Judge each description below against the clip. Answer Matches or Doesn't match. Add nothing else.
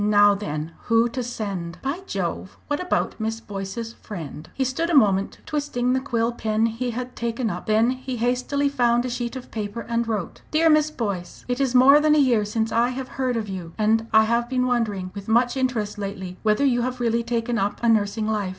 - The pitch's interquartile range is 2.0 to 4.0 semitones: Matches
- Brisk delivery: Matches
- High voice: Matches